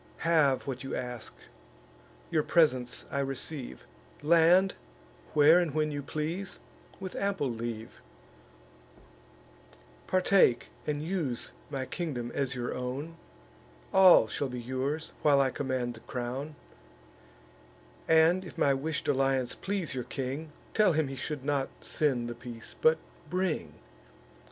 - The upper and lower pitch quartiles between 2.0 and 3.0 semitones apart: No, average, 4.0 semitones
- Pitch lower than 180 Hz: Yes, medium, 140 Hz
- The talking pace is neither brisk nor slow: No, slow, 125 wpm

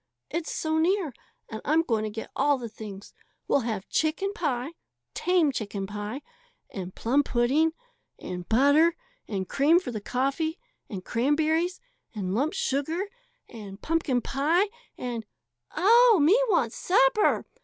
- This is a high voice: Yes, very high, 280 Hz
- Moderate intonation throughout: No, wide, 6.7 semitones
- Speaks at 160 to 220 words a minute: No, average, 145 wpm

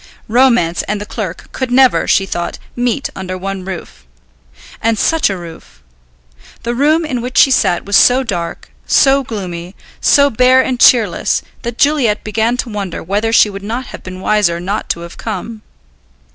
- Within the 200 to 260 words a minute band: No, average, 170 wpm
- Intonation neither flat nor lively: Yes, average, 5.0 semitones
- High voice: Yes, high, 215 Hz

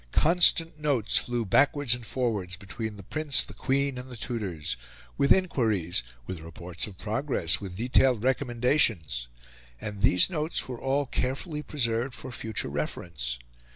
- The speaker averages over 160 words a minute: No, average, 145 wpm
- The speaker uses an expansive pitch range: Yes, wide, 6.9 semitones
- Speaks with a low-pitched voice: Yes, low, 120 Hz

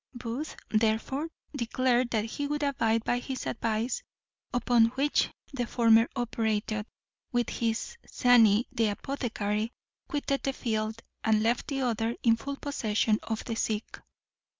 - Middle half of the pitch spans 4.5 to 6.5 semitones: No, narrow, 2.6 semitones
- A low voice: No, high, 230 Hz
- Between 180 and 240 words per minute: No, slow, 135 wpm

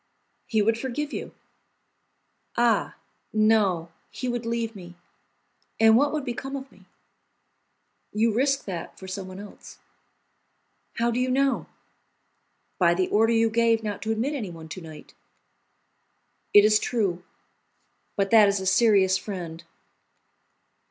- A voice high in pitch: Yes, high, 220 Hz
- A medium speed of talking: No, slow, 130 wpm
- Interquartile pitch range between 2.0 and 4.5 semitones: Yes, average, 3.9 semitones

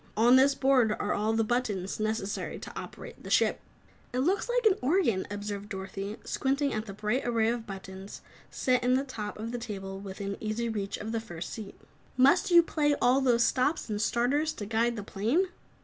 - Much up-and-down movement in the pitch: No, average, 4.2 semitones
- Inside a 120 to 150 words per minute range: No, average, 195 wpm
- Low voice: No, high, 225 Hz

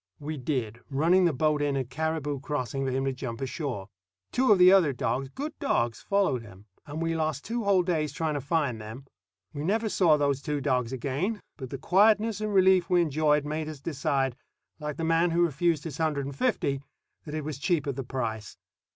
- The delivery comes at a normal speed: No, fast, 210 wpm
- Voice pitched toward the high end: No, medium, 150 Hz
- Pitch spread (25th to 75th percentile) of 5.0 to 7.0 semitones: No, average, 4.2 semitones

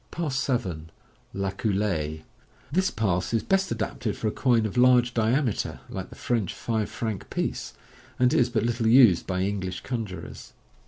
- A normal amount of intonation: Yes, average, 4.3 semitones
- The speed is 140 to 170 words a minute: Yes, average, 165 wpm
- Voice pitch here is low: Yes, low, 110 Hz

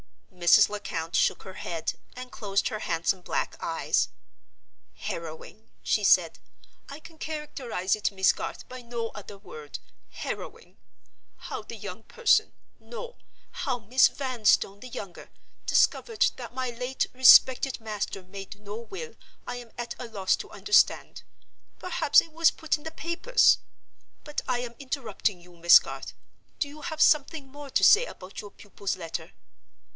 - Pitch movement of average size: No, wide, 6.8 semitones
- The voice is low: No, high, 240 Hz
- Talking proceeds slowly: No, average, 145 wpm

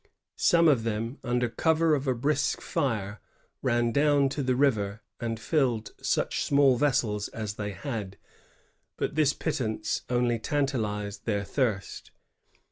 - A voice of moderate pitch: No, low, 120 Hz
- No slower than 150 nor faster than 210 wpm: No, slow, 135 wpm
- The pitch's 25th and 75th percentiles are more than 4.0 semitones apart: Yes, average, 4.7 semitones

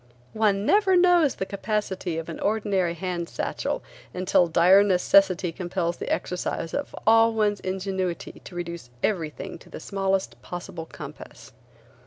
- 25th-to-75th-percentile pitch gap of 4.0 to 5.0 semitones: No, average, 3.0 semitones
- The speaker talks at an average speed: Yes, average, 145 wpm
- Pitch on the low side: No, high, 190 Hz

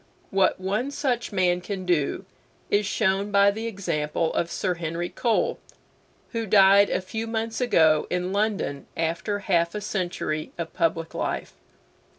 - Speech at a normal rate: Yes, average, 150 wpm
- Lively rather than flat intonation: No, average, 3.8 semitones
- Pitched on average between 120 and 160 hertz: No, high, 190 Hz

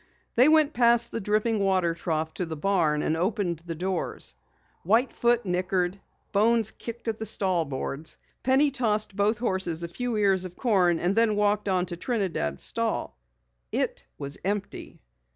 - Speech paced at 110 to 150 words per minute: No, average, 165 wpm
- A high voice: Yes, high, 195 Hz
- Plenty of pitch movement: No, average, 4.6 semitones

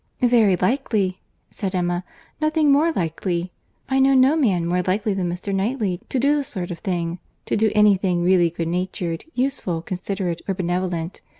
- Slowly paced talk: No, average, 165 wpm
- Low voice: No, high, 190 Hz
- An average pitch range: No, wide, 5.7 semitones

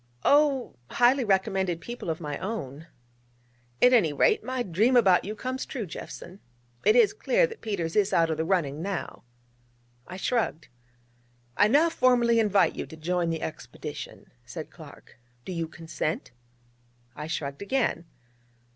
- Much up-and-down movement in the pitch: Yes, wide, 7.0 semitones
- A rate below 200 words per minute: Yes, average, 150 wpm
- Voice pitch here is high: Yes, high, 195 Hz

